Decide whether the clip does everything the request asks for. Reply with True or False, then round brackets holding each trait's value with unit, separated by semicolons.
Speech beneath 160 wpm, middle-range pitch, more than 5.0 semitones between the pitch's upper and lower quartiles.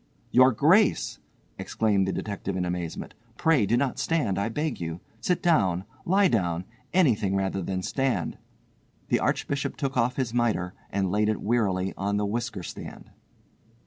False (150 wpm; 110 Hz; 5.4 semitones)